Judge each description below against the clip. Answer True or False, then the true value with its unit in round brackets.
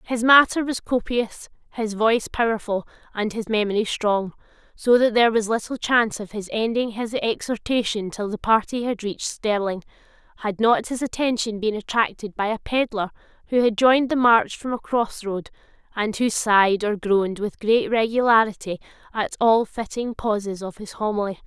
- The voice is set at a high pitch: True (220 Hz)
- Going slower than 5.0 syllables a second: False (5.1 syllables/s)